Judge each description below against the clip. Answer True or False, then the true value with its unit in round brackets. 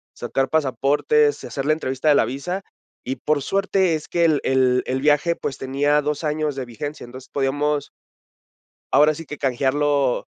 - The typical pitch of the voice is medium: True (145 Hz)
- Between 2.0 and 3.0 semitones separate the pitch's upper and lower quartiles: True (2.4 semitones)